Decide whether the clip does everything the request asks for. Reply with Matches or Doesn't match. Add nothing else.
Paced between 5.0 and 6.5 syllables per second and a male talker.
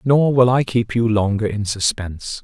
Doesn't match